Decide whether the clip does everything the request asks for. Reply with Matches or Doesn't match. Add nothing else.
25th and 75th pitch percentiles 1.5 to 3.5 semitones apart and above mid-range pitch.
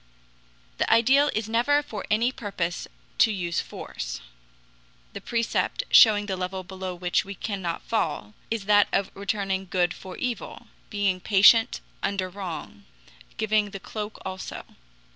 Matches